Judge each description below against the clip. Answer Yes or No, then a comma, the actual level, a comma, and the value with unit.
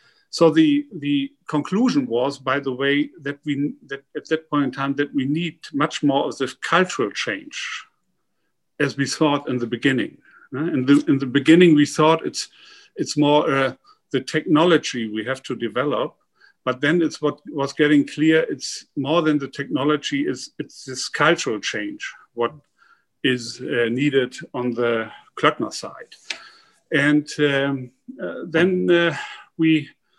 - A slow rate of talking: No, average, 155 wpm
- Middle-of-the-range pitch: Yes, medium, 145 Hz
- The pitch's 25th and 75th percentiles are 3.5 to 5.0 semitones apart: No, narrow, 2.6 semitones